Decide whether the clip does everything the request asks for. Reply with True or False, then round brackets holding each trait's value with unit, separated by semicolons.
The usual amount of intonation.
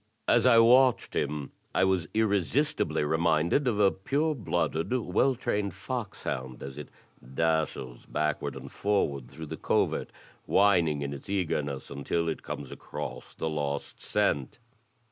False (6.9 semitones)